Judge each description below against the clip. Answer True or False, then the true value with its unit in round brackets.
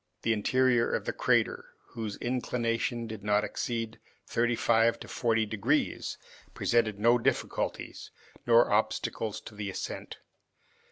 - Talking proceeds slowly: True (125 wpm)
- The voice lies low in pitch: True (115 Hz)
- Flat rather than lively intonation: True (1.6 semitones)